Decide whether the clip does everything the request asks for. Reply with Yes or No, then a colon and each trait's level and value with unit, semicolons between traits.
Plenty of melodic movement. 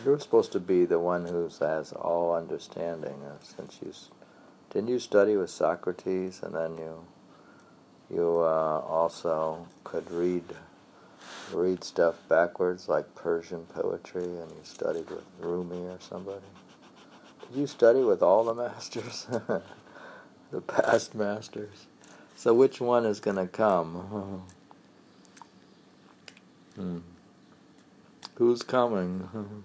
No: average, 4.1 semitones